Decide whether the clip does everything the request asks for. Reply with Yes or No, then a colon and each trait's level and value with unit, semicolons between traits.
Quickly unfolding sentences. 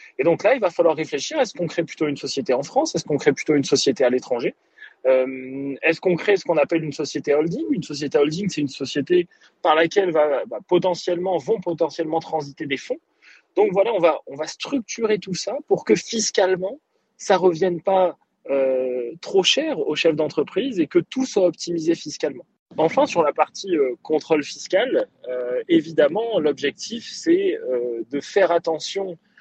No: average, 185 wpm